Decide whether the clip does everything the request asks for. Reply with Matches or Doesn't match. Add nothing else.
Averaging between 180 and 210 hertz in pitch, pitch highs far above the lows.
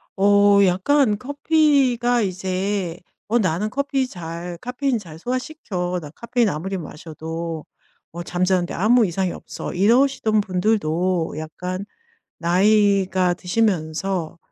Doesn't match